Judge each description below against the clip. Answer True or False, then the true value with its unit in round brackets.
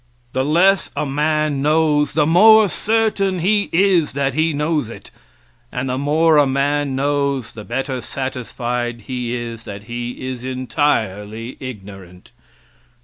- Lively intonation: False (4.4 semitones)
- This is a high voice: False (140 Hz)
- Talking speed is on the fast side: False (140 wpm)